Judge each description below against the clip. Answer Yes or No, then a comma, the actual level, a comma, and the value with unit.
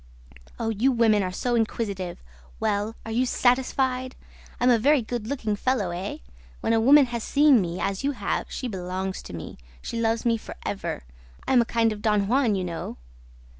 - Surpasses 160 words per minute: Yes, average, 195 wpm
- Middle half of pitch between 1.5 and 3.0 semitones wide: No, average, 3.9 semitones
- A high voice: Yes, high, 225 Hz